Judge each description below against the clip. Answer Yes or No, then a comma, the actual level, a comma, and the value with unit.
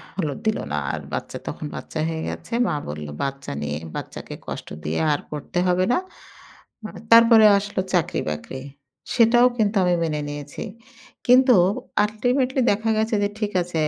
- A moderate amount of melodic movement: No, wide, 7.3 semitones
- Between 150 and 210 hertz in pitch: Yes, medium, 185 Hz